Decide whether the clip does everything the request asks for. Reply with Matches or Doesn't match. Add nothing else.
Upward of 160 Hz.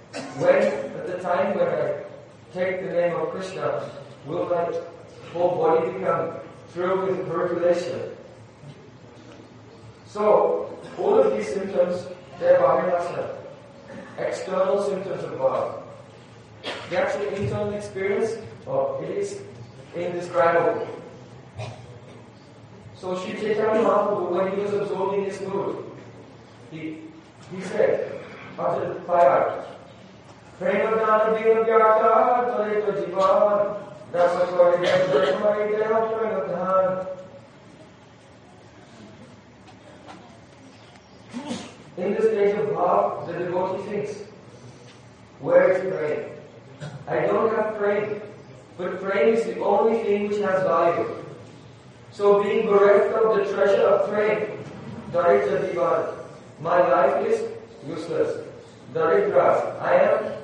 Matches